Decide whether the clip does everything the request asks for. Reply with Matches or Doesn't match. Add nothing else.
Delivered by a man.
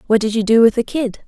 Doesn't match